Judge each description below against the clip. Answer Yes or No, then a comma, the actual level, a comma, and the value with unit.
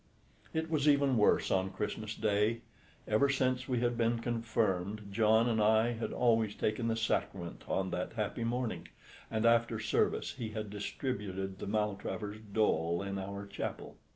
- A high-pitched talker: No, low, 110 Hz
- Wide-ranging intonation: No, average, 2.7 semitones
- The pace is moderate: Yes, average, 155 wpm